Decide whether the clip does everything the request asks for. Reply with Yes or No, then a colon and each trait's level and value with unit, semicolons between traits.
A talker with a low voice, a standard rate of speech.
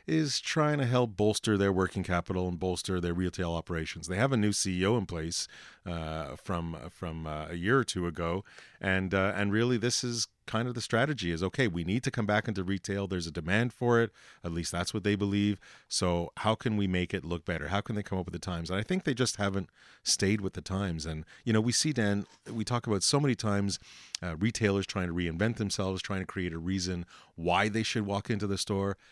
No: low, 100 Hz; fast, 235 wpm